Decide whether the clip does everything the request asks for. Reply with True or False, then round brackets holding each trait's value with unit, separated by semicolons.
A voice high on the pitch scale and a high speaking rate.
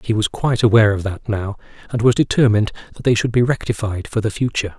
False (110 Hz; 225 wpm)